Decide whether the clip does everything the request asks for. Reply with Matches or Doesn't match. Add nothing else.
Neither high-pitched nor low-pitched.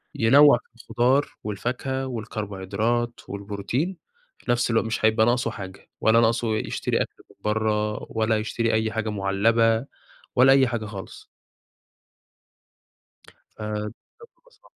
Doesn't match